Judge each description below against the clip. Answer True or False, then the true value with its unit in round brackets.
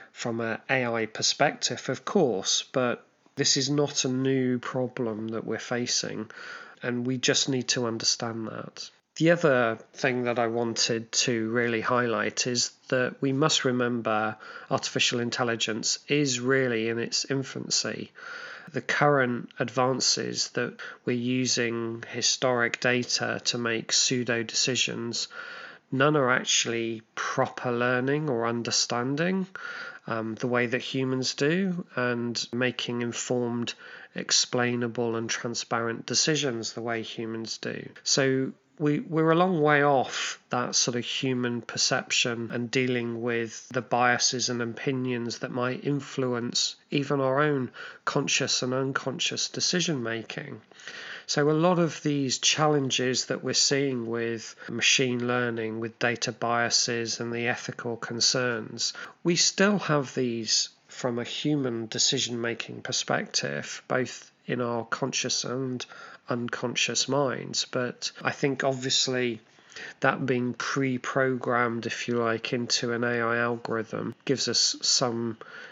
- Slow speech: True (130 wpm)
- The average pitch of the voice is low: True (125 Hz)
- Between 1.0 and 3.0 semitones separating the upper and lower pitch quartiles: True (2.4 semitones)